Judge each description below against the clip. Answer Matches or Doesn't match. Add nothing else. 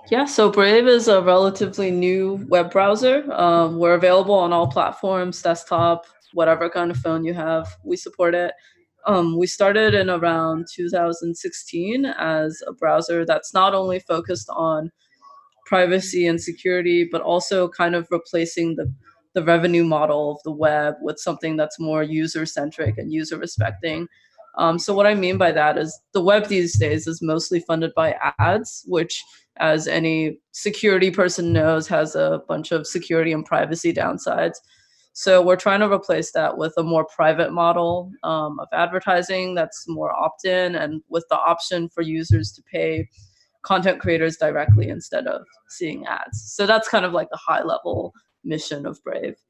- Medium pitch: Matches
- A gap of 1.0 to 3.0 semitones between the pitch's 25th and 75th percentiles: Matches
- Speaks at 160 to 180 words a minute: Matches